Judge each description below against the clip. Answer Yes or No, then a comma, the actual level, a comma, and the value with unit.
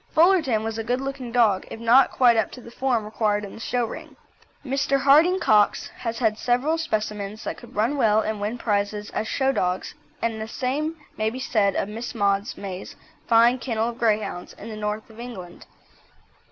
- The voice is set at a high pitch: Yes, high, 225 Hz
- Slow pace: No, average, 195 wpm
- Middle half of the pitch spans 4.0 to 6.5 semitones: No, average, 3.1 semitones